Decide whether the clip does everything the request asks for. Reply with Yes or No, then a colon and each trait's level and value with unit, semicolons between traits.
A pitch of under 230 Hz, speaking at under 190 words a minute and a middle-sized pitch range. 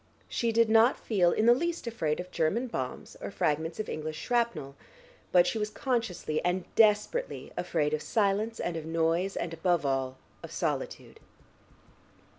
No: medium, 185 Hz; average, 160 wpm; wide, 6.2 semitones